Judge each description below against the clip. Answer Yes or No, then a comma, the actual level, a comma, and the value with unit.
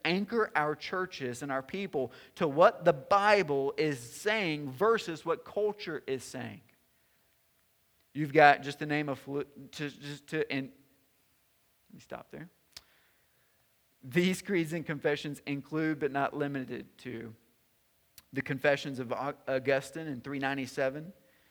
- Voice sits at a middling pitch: Yes, medium, 145 Hz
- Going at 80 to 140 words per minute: Yes, slow, 135 wpm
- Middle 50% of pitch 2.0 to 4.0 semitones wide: Yes, average, 3.5 semitones